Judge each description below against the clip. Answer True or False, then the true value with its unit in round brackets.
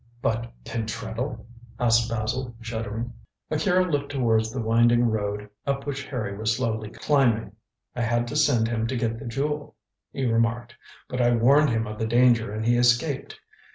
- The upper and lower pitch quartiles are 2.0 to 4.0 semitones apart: True (2.4 semitones)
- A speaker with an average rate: True (165 wpm)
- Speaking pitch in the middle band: False (120 Hz)